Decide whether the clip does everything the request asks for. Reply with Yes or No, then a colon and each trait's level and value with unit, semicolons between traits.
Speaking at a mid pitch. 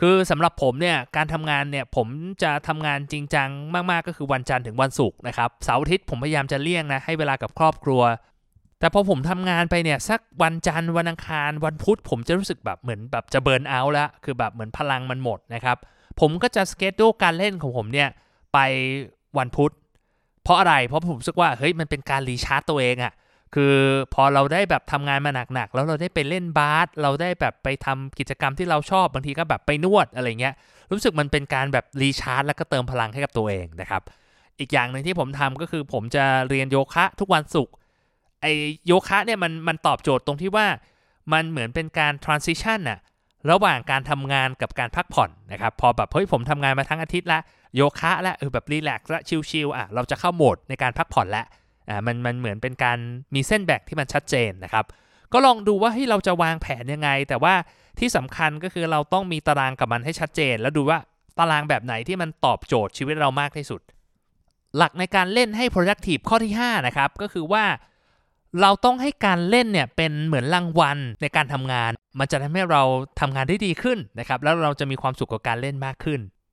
Yes: medium, 145 Hz